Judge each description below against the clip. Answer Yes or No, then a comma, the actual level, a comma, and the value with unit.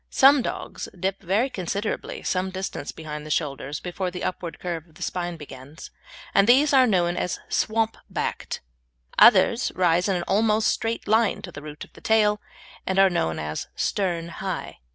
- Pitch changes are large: No, average, 4.2 semitones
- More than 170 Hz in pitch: Yes, medium, 185 Hz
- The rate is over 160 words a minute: Yes, average, 175 wpm